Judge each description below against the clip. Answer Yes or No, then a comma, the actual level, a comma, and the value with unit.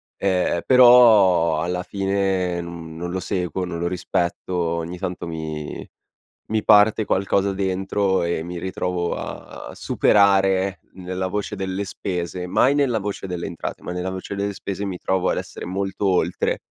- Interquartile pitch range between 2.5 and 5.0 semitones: No, narrow, 2.0 semitones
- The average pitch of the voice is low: Yes, very low, 95 Hz